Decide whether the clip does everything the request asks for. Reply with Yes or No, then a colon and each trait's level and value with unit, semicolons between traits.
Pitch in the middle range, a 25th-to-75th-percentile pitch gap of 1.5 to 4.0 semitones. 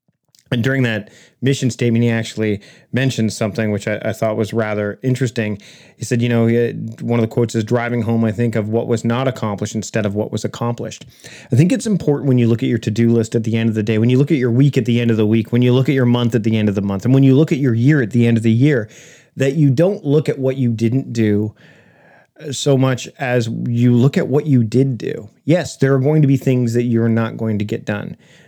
No: low, 120 Hz; average, 2.8 semitones